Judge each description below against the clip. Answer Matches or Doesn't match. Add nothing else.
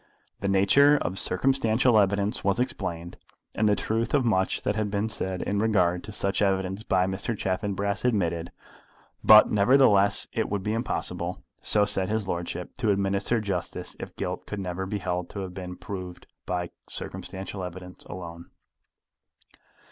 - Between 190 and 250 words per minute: Doesn't match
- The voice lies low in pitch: Matches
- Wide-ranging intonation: Doesn't match